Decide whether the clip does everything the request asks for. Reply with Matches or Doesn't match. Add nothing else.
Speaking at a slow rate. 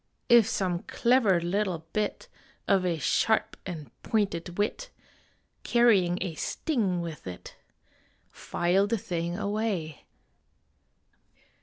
Matches